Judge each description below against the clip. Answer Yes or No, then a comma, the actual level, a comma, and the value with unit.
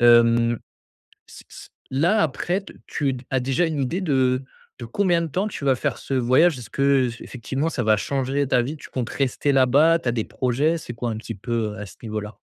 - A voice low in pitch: Yes, low, 130 Hz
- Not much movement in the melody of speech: No, average, 4.0 semitones